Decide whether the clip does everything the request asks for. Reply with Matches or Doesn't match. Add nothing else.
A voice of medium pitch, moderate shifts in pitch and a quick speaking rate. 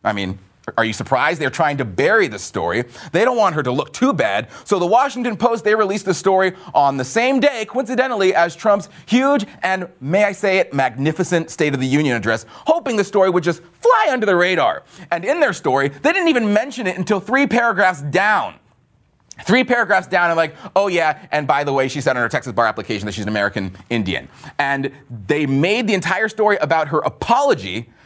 Doesn't match